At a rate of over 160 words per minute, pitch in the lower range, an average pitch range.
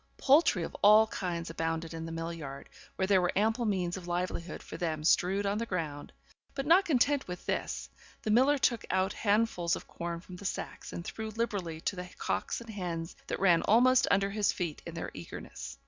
No: fast, 205 wpm; medium, 185 Hz; average, 4.6 semitones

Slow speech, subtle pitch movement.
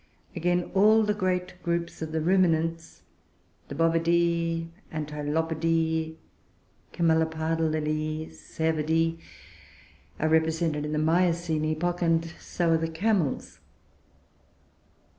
Yes: slow, 100 wpm; narrow, 1.4 semitones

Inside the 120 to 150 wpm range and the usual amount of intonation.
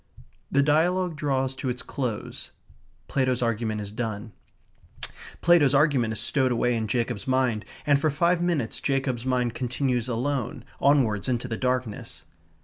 Yes: average, 140 wpm; average, 3.3 semitones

